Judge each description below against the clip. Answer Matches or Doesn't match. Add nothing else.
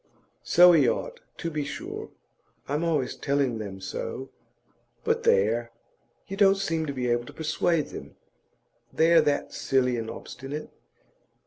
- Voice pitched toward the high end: Doesn't match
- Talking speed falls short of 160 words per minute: Matches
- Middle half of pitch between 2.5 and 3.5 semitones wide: Doesn't match